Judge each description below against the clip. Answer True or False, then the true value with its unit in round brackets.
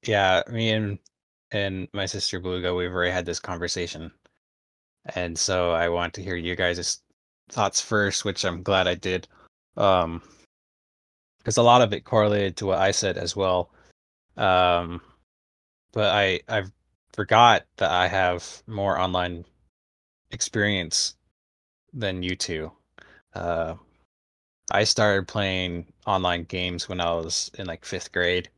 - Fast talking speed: False (140 wpm)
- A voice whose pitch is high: False (90 Hz)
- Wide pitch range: False (2.5 semitones)